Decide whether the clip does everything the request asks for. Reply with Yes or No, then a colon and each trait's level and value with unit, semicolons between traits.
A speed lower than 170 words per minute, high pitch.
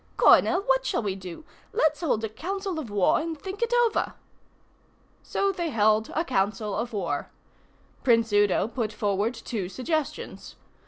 Yes: average, 155 wpm; high, 235 Hz